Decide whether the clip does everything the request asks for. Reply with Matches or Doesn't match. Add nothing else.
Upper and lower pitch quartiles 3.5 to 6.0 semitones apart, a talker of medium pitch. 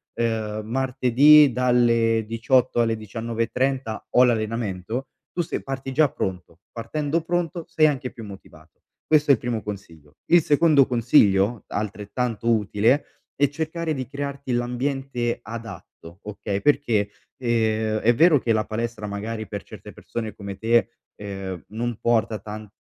Doesn't match